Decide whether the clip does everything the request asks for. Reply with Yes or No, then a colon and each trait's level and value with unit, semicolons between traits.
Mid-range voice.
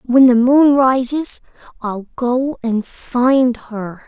No: very high, 250 Hz